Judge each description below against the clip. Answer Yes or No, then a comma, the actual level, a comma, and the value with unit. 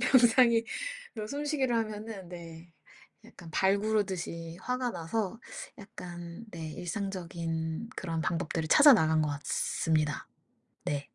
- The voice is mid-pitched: Yes, medium, 180 Hz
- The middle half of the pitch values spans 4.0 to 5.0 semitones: No, wide, 5.5 semitones